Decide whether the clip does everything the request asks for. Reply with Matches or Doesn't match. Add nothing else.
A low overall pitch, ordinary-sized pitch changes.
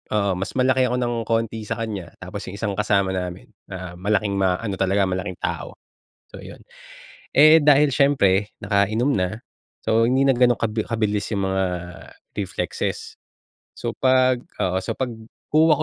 Matches